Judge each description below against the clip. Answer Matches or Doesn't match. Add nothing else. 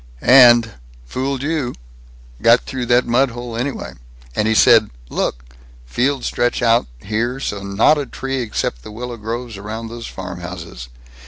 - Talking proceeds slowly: Doesn't match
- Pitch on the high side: Doesn't match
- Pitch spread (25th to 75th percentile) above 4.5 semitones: Doesn't match